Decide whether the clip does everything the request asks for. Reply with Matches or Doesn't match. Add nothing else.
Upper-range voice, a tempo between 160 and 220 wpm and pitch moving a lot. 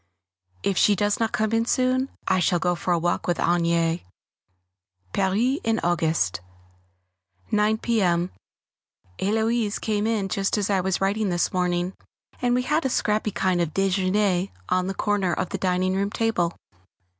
Doesn't match